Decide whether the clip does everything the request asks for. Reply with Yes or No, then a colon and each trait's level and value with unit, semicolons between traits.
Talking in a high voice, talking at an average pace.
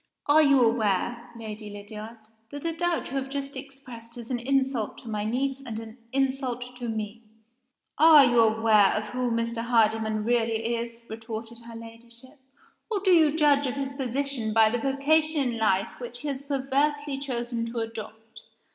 Yes: high, 240 Hz; average, 175 wpm